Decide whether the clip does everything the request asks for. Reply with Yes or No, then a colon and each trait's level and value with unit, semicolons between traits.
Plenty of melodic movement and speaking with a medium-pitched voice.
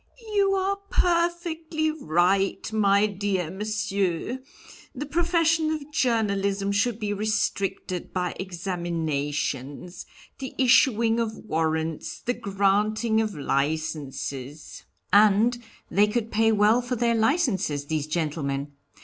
No: wide, 6.1 semitones; high, 205 Hz